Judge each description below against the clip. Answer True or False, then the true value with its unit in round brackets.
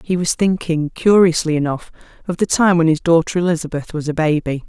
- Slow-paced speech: False (190 wpm)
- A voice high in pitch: False (165 Hz)